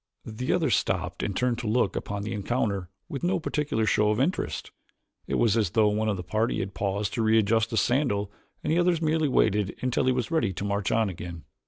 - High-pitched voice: No, low, 110 Hz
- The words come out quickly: Yes, fast, 220 wpm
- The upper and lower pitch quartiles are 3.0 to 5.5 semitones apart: Yes, average, 4.0 semitones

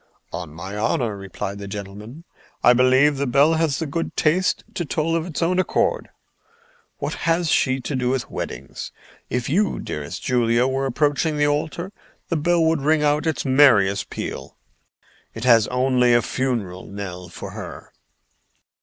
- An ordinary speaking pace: Yes, average, 165 wpm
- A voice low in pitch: Yes, low, 130 Hz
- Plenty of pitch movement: Yes, wide, 6.2 semitones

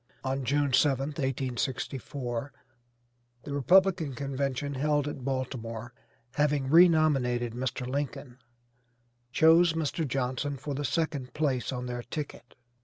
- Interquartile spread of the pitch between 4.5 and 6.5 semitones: No, average, 2.7 semitones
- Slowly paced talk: Yes, slow, 115 wpm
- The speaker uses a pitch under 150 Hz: Yes, low, 135 Hz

